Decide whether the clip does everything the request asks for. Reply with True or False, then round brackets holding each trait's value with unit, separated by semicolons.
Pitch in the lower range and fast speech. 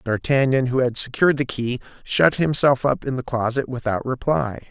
False (130 Hz; 180 wpm)